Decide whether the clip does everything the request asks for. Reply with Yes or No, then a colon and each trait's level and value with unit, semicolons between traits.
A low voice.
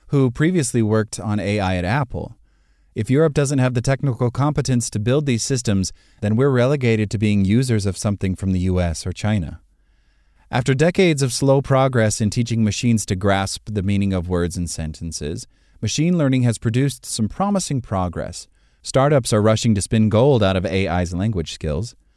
Yes: low, 110 Hz